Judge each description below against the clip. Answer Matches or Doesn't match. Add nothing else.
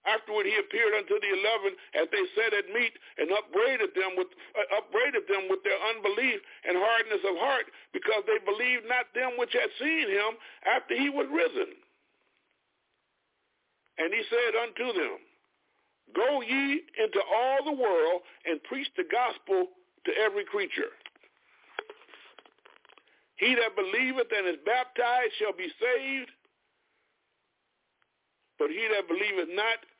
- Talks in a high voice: Matches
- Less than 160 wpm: Matches